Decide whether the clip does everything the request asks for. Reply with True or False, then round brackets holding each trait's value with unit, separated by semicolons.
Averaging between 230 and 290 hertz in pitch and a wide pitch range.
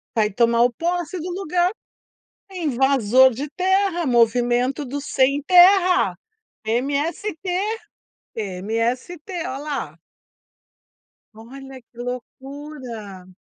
True (270 Hz; 6.0 semitones)